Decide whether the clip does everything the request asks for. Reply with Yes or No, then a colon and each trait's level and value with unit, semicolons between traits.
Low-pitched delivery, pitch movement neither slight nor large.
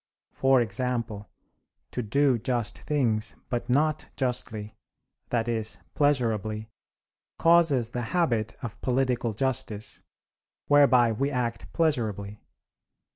Yes: low, 120 Hz; average, 3.5 semitones